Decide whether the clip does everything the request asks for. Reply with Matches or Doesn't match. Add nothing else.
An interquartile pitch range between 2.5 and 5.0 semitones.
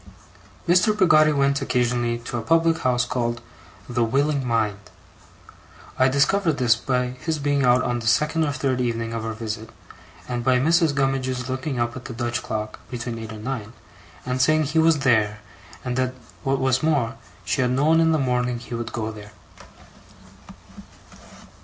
Matches